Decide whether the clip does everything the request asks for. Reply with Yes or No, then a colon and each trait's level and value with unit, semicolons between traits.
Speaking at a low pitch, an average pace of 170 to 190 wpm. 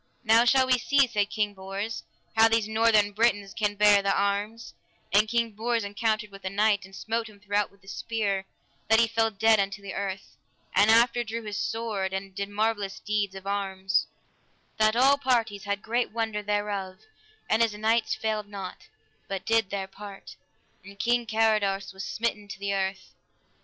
No: high, 210 Hz; average, 180 wpm